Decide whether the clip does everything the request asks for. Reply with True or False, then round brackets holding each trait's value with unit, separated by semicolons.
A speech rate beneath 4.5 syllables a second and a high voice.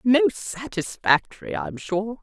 True (4.3 syllables/s; 200 Hz)